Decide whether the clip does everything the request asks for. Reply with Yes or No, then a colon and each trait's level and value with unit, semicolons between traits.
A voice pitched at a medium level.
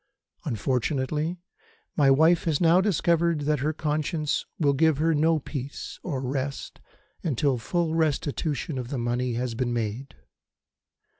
Yes: medium, 145 Hz